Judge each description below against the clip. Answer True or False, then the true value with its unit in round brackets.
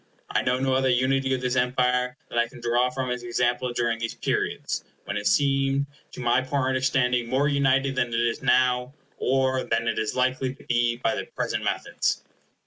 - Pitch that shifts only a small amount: True (1.7 semitones)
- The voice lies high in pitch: False (125 Hz)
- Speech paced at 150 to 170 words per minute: False (200 wpm)